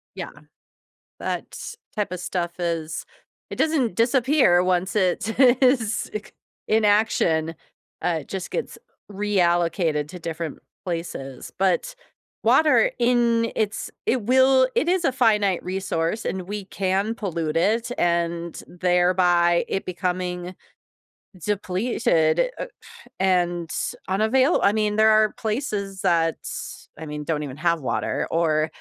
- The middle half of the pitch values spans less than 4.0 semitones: No, average, 4.5 semitones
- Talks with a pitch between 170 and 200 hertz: Yes, high, 190 Hz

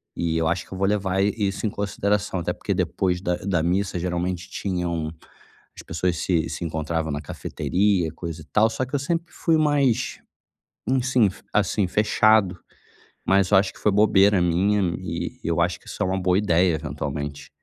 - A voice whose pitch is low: Yes, very low, 95 Hz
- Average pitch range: Yes, average, 3.4 semitones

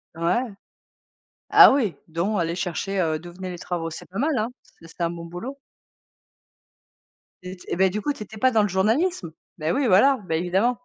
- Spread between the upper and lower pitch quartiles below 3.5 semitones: No, average, 5.0 semitones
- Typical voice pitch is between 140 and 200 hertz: Yes, high, 190 Hz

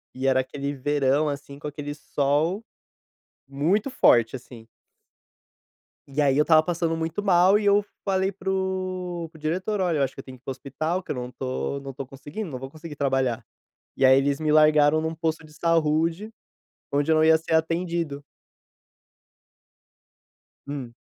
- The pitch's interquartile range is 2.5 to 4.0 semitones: Yes, average, 3.7 semitones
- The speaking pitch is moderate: Yes, medium, 155 Hz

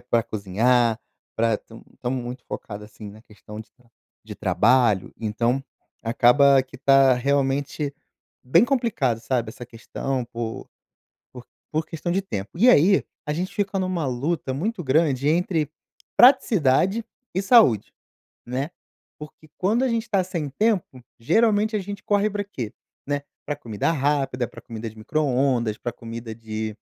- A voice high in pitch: No, low, 135 Hz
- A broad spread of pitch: Yes, wide, 7.1 semitones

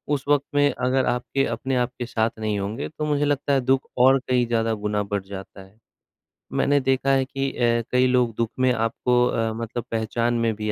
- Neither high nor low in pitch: No, low, 120 Hz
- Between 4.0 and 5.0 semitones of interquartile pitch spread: No, average, 3.0 semitones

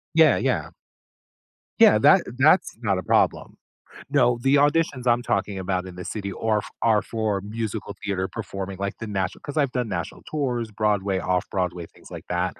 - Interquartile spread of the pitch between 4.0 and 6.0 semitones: Yes, average, 4.4 semitones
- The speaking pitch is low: Yes, low, 105 Hz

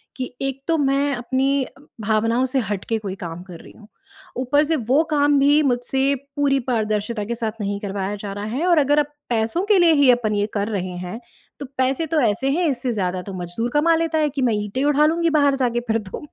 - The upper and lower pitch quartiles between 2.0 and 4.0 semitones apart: No, average, 5.2 semitones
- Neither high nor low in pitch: No, very high, 255 Hz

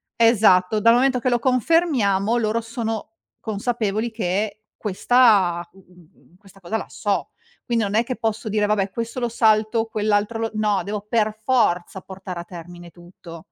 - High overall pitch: Yes, high, 215 Hz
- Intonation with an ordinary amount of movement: Yes, average, 3.1 semitones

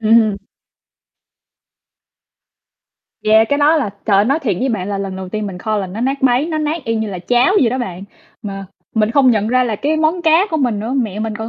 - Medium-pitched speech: No, high, 225 Hz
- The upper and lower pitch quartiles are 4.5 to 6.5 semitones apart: Yes, average, 5.0 semitones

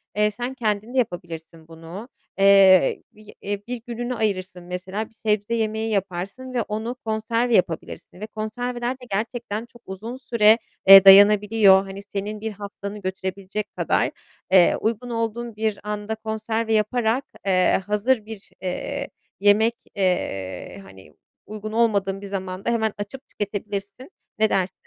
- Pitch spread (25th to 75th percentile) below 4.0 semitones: Yes, narrow, 2.6 semitones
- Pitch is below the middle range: No, high, 210 Hz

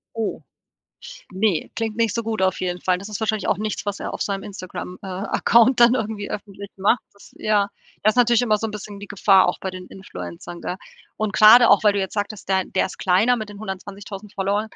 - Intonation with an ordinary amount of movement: No, narrow, 2.2 semitones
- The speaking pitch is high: Yes, high, 205 Hz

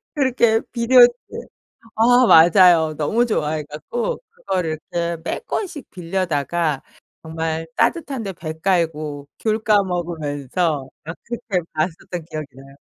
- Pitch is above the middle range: No, medium, 170 Hz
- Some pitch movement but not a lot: No, wide, 6.1 semitones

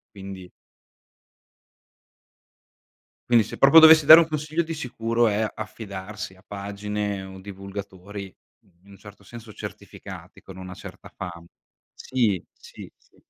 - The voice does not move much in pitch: No, average, 3.4 semitones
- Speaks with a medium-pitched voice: No, low, 105 Hz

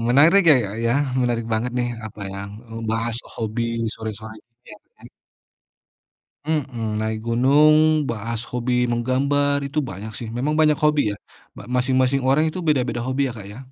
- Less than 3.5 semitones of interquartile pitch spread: No, average, 4.0 semitones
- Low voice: Yes, low, 125 Hz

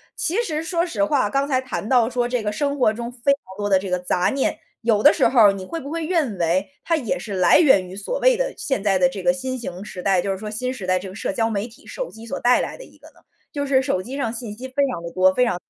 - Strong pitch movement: Yes, wide, 6.0 semitones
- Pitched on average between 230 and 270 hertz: Yes, high, 235 Hz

